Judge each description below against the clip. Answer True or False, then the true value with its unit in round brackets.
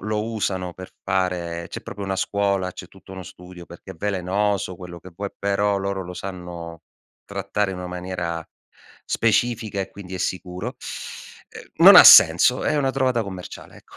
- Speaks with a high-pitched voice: False (95 Hz)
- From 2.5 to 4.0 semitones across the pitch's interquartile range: False (2.1 semitones)